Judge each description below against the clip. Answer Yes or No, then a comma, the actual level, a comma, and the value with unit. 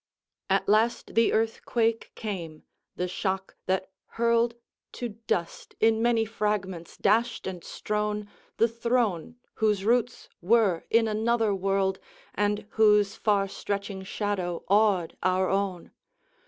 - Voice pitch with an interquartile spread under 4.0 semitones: Yes, average, 2.9 semitones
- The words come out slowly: Yes, slow, 125 wpm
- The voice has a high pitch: Yes, high, 210 Hz